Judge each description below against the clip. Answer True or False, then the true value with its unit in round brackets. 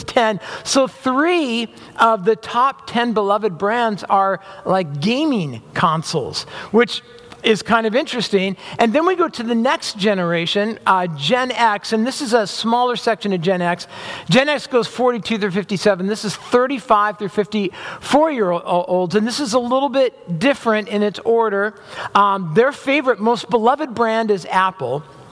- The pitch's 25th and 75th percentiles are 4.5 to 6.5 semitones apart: False (3.8 semitones)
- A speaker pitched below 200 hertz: False (225 Hz)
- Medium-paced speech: True (165 wpm)